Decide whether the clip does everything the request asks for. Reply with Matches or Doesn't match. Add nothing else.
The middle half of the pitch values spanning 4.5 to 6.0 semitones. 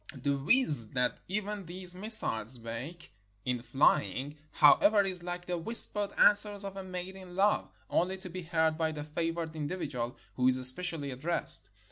Matches